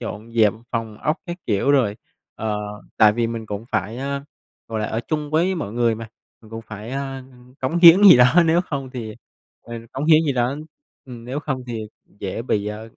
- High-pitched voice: No, low, 120 Hz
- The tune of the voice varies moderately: Yes, average, 4.1 semitones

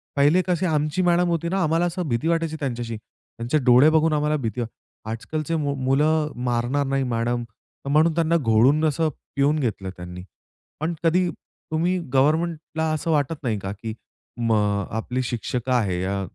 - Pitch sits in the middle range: Yes, medium, 145 Hz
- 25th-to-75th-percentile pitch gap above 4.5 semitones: Yes, average, 5.3 semitones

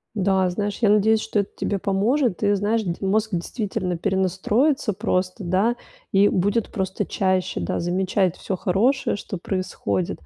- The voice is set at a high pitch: Yes, high, 195 Hz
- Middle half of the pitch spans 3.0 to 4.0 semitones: No, narrow, 2.6 semitones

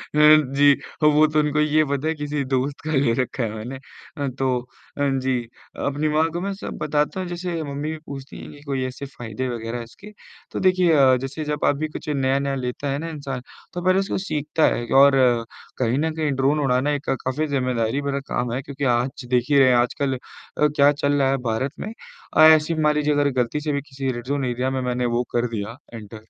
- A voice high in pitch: No, medium, 140 Hz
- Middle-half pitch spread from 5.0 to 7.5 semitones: No, average, 2.9 semitones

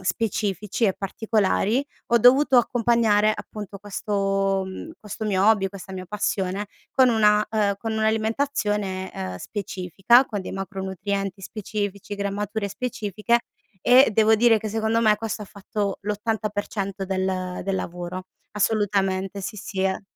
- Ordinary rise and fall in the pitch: No, narrow, 2.2 semitones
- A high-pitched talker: Yes, high, 205 Hz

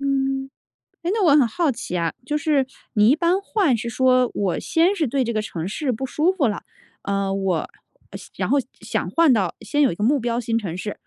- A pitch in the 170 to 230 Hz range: No, very high, 255 Hz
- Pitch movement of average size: No, wide, 6.0 semitones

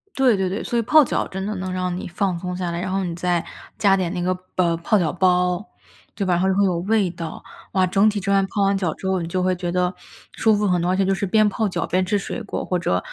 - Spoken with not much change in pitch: Yes, narrow, 1.8 semitones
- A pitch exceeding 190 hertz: No, medium, 185 Hz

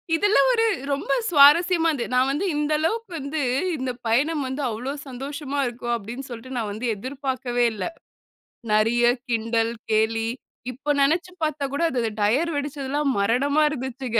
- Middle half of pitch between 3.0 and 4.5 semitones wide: Yes, average, 3.9 semitones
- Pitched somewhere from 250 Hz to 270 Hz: Yes, very high, 265 Hz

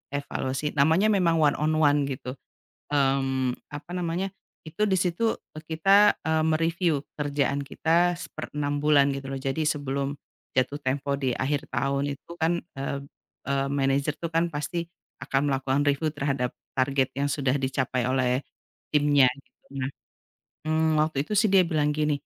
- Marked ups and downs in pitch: No, average, 2.8 semitones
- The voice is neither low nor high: Yes, medium, 145 Hz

